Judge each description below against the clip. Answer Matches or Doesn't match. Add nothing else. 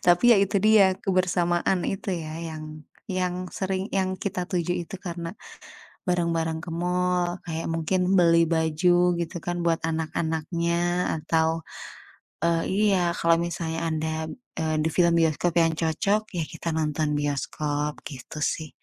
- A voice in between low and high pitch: Matches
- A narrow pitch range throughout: Matches